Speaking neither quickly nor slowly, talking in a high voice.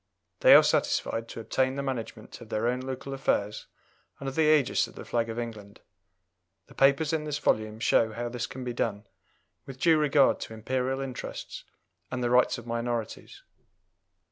No: average, 175 wpm; low, 125 Hz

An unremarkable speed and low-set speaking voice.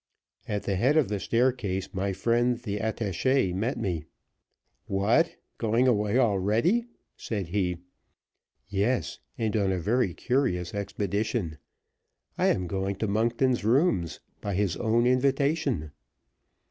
No: slow, 125 wpm; low, 105 Hz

